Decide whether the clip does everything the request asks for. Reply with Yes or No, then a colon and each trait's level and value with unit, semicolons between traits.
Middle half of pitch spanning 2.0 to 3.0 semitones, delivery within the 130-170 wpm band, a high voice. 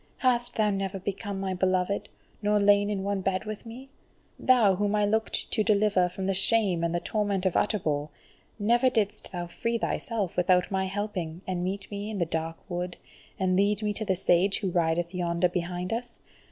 No: average, 2.7 semitones; average, 195 wpm; high, 195 Hz